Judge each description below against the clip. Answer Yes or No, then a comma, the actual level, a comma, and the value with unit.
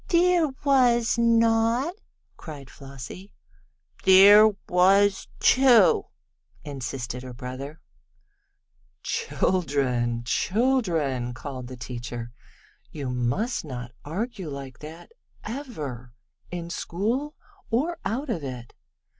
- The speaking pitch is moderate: Yes, medium, 170 Hz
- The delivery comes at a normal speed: No, slow, 90 wpm